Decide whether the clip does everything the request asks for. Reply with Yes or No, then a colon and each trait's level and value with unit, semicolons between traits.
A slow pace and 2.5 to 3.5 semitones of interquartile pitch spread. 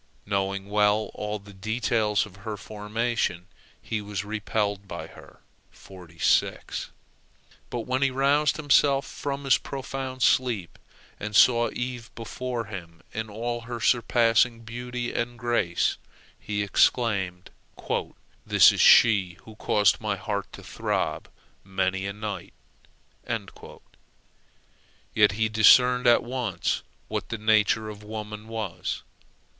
Yes: slow, 120 wpm; average, 2.9 semitones